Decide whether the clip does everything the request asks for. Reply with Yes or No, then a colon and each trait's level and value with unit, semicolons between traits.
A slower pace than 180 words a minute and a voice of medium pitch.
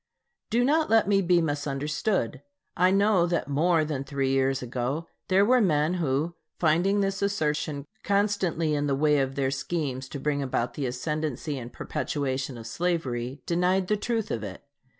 Yes: average, 170 wpm; medium, 150 Hz